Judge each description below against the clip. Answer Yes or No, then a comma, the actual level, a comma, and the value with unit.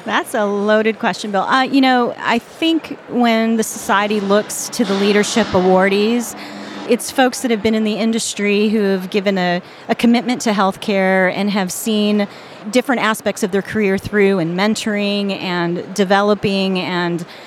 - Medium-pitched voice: No, high, 210 Hz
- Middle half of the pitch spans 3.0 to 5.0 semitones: No, narrow, 2.6 semitones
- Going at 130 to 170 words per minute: Yes, average, 165 wpm